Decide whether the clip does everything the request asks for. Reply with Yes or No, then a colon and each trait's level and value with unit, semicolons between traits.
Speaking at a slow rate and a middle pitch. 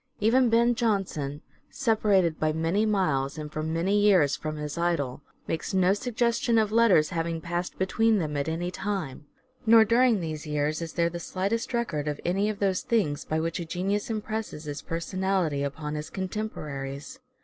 No: average, 170 wpm; medium, 175 Hz